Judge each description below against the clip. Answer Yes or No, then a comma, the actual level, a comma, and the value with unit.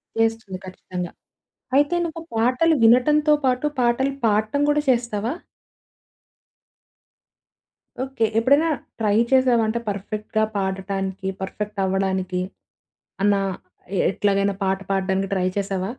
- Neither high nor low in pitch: No, high, 215 Hz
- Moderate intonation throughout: Yes, average, 4.6 semitones